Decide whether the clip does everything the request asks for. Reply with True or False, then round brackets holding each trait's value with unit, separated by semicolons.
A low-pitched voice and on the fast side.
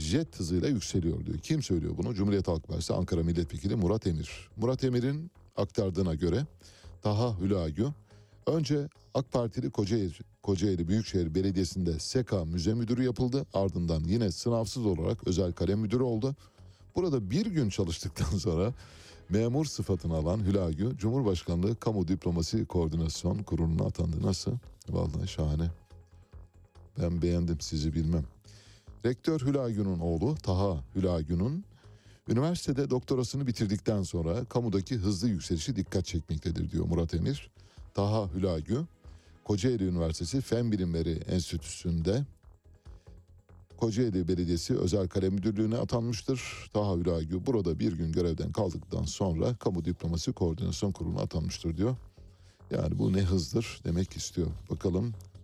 False (95 Hz; 120 wpm)